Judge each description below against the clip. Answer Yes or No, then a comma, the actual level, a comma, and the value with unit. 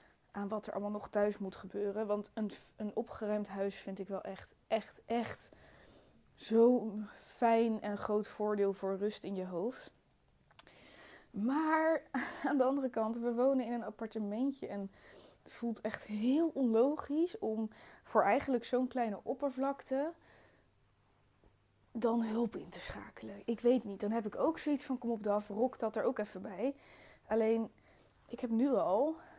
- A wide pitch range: No, average, 3.5 semitones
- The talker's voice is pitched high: Yes, high, 225 Hz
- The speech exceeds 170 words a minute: No, average, 160 wpm